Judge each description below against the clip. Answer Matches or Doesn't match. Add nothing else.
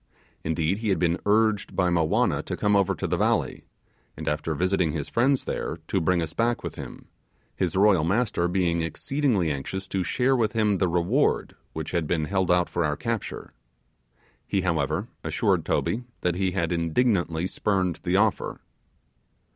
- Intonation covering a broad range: Doesn't match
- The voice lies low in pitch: Matches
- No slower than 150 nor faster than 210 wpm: Matches